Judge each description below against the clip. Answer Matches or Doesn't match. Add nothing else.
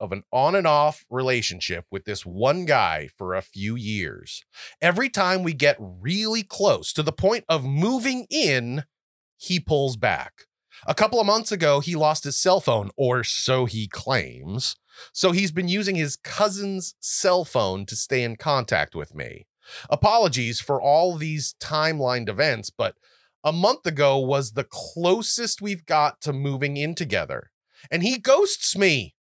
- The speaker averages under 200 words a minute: Matches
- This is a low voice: Doesn't match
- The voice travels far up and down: Matches